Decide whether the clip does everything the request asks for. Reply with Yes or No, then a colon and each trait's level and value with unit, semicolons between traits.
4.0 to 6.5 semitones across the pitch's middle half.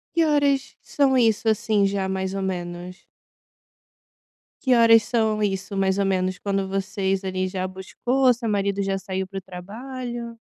No: average, 3.4 semitones